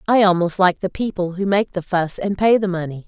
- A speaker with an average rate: No, fast, 255 wpm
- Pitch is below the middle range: No, medium, 185 Hz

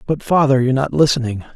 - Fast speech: No, average, 195 wpm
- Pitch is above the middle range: No, low, 135 Hz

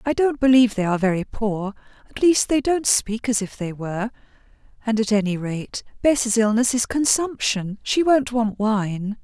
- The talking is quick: No, average, 170 wpm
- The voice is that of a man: No, female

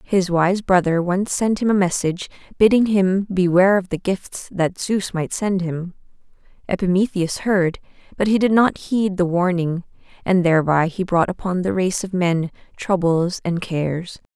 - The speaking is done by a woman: Yes, female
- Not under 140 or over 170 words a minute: Yes, average, 165 wpm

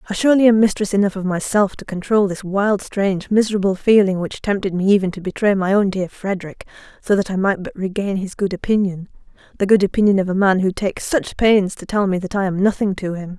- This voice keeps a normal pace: No, fast, 230 wpm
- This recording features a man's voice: No, female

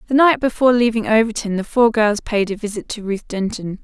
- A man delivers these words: No, female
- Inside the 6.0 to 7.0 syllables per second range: No, 5.8 syllables/s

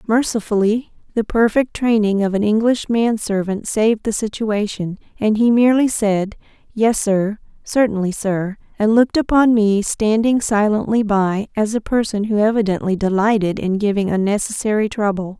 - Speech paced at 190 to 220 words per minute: No, average, 140 wpm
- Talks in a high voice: Yes, high, 215 Hz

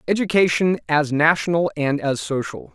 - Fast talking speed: No, slow, 130 wpm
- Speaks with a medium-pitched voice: Yes, medium, 155 Hz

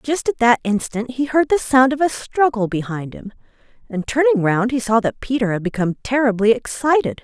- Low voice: No, high, 240 Hz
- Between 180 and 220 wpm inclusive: Yes, average, 200 wpm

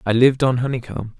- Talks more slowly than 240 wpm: Yes, average, 200 wpm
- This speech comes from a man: Yes, male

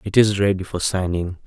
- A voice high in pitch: No, very low, 95 Hz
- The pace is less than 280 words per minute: Yes, fast, 205 wpm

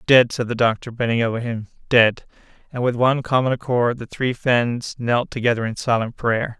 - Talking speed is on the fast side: No, average, 190 wpm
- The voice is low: Yes, low, 120 Hz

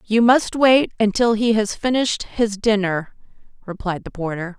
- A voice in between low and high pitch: No, high, 215 Hz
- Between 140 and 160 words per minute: Yes, average, 155 wpm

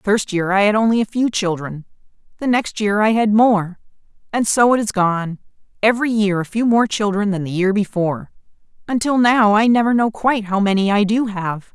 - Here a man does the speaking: No, female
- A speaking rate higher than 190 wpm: Yes, average, 200 wpm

